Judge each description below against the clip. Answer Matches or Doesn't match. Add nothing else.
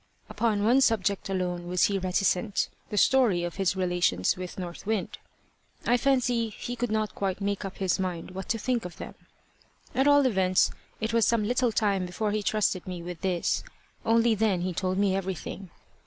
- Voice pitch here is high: Matches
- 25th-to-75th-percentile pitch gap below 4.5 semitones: Matches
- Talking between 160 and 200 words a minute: Matches